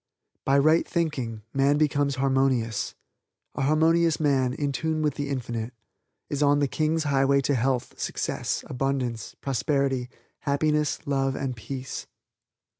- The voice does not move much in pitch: Yes, narrow, 2.2 semitones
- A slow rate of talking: Yes, slow, 130 wpm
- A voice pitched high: No, medium, 140 Hz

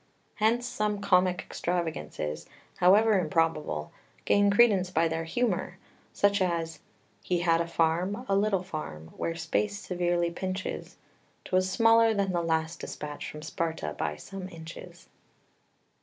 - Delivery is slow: Yes, slow, 130 wpm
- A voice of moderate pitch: Yes, medium, 175 Hz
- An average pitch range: Yes, average, 3.6 semitones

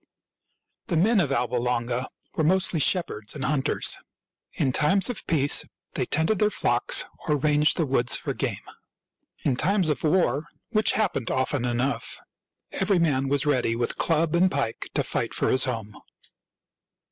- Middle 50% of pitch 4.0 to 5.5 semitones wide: Yes, average, 5.1 semitones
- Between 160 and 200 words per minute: Yes, average, 165 wpm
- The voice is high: No, medium, 145 Hz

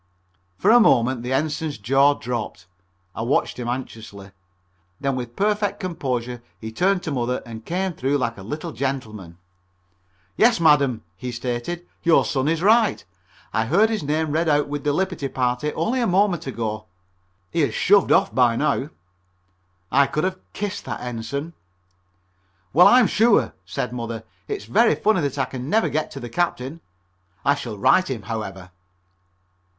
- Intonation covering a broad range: Yes, wide, 6.5 semitones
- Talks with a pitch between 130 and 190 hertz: Yes, medium, 140 Hz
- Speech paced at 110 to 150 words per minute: No, average, 165 wpm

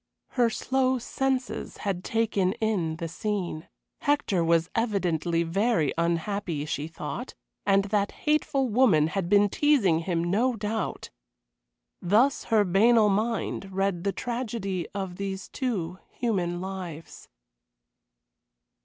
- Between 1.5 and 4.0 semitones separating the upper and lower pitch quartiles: No, average, 4.8 semitones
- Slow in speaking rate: Yes, slow, 120 wpm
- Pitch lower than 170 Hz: No, high, 195 Hz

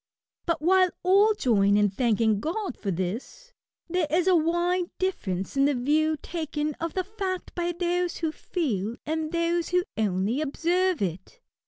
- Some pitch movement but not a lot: No, wide, 7.4 semitones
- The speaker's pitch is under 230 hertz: No, very high, 320 Hz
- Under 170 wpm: Yes, average, 160 wpm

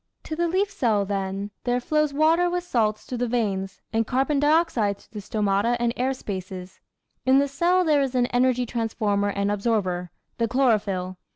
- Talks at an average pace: Yes, average, 180 wpm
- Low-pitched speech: No, high, 235 Hz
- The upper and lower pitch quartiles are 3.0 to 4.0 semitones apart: No, wide, 5.5 semitones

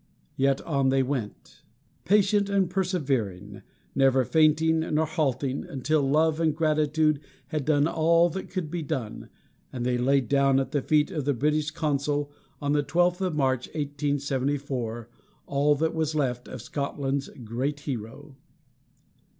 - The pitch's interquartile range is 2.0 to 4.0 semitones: Yes, average, 2.8 semitones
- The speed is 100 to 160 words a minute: Yes, average, 145 wpm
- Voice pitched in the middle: Yes, medium, 145 Hz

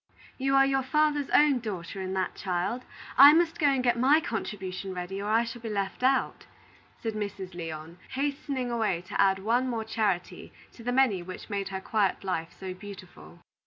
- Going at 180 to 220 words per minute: Yes, average, 190 wpm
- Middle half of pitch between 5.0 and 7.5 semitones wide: Yes, wide, 5.5 semitones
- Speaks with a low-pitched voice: No, high, 215 Hz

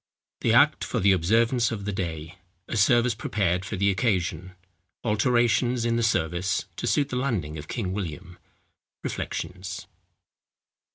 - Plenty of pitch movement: No, average, 4.6 semitones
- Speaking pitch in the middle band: No, very low, 95 Hz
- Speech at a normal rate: No, slow, 125 wpm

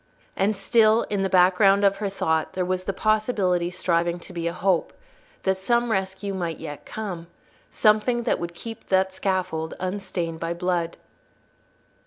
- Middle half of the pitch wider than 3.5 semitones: No, average, 2.8 semitones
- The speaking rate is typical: Yes, average, 160 wpm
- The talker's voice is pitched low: No, high, 190 Hz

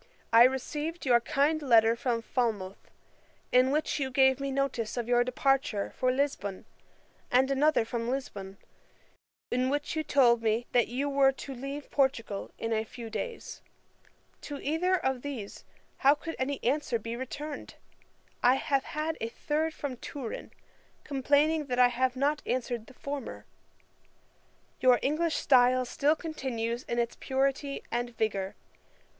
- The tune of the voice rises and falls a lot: No, average, 3.2 semitones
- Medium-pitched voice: No, very high, 260 Hz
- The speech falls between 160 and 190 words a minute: No, average, 150 wpm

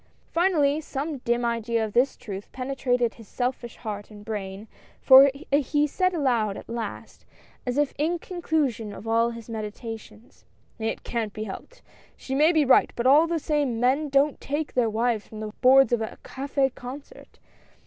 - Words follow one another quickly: No, average, 175 wpm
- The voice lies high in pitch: Yes, very high, 250 Hz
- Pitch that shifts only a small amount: No, average, 4.3 semitones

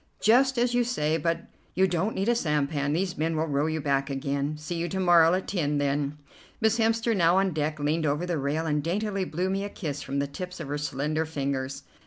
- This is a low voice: No, medium, 160 Hz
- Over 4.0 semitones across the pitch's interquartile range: Yes, average, 4.6 semitones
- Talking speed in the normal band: No, fast, 230 wpm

